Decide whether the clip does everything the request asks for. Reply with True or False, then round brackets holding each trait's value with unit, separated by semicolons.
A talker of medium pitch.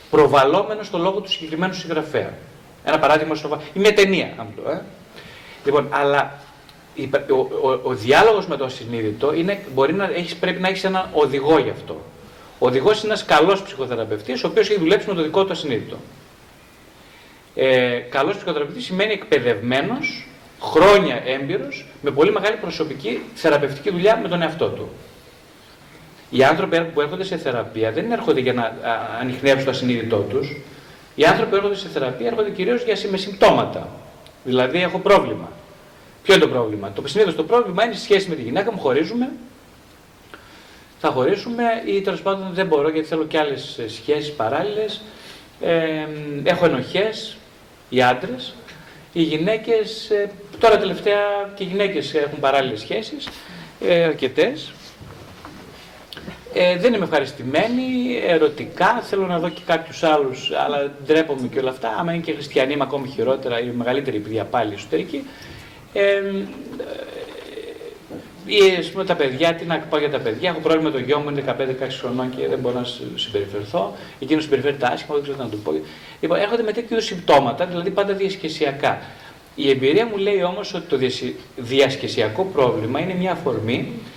True (170 Hz)